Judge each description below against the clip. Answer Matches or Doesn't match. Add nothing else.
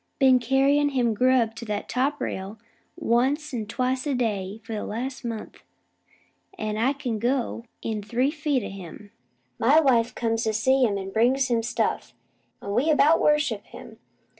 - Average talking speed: Matches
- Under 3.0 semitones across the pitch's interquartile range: Doesn't match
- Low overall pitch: Doesn't match